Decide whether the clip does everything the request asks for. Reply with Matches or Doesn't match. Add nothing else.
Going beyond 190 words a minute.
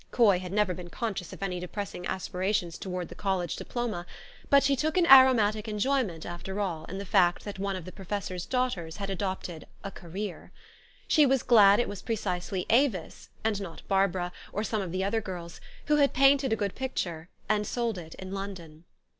Matches